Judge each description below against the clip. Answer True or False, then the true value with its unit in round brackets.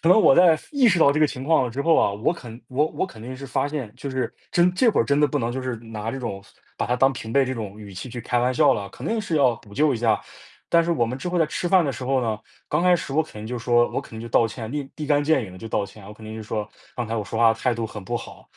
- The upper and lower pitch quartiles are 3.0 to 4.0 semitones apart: False (5.0 semitones)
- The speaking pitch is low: True (125 Hz)